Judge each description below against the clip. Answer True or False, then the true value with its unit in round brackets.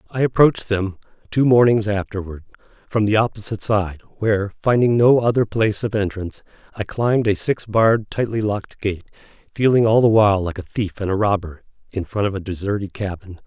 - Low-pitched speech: True (105 Hz)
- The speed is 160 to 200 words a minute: True (175 wpm)